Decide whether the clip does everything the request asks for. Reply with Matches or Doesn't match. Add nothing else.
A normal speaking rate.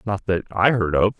Doesn't match